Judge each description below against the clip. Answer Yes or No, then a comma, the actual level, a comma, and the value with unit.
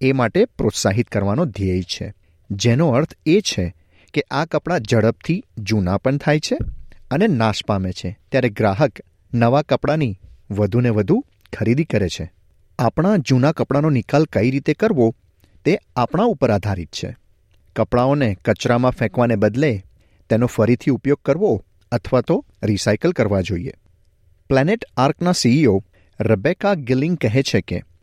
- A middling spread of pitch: No, wide, 6.0 semitones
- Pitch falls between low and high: No, low, 115 Hz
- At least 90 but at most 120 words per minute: No, average, 135 wpm